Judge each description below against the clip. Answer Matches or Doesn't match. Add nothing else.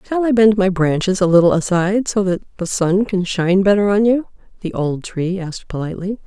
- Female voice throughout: Matches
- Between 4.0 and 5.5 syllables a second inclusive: Doesn't match